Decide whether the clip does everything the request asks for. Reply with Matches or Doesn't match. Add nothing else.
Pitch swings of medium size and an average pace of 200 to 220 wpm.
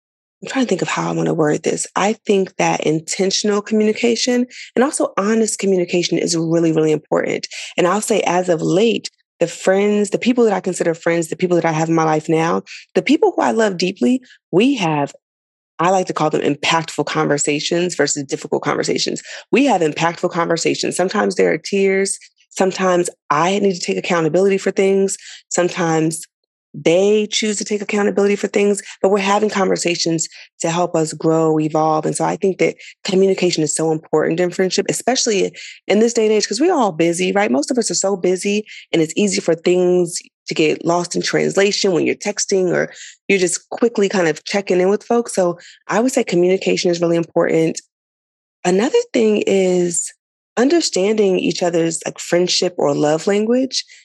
Doesn't match